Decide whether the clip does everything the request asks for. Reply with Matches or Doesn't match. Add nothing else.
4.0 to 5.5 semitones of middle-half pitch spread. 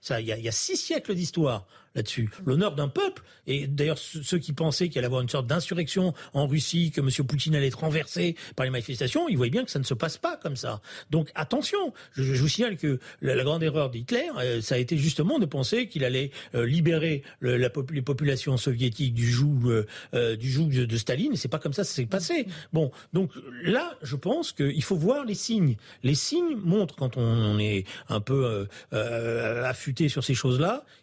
Matches